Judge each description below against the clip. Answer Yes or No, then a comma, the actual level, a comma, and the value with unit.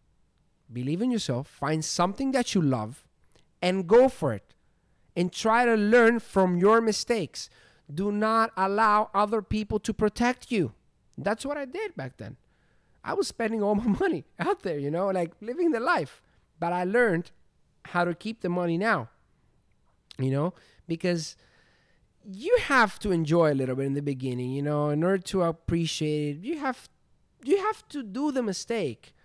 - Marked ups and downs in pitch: Yes, wide, 5.9 semitones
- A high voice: Yes, high, 195 Hz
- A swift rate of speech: No, average, 170 wpm